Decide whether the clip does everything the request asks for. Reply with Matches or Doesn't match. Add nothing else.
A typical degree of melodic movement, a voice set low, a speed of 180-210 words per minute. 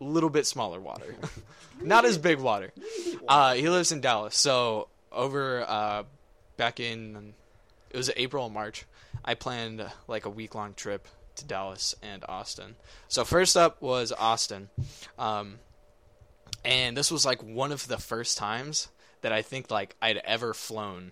Doesn't match